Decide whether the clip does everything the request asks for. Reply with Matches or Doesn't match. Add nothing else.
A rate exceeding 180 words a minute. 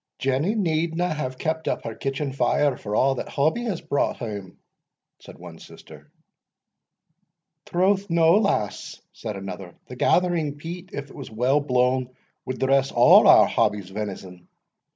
Doesn't match